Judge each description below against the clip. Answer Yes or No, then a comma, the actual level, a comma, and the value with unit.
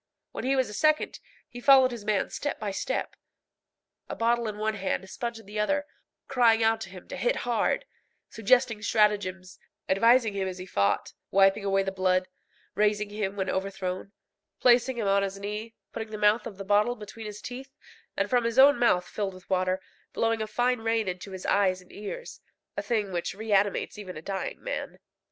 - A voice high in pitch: Yes, high, 210 Hz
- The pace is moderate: Yes, average, 195 wpm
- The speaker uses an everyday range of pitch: Yes, average, 3.2 semitones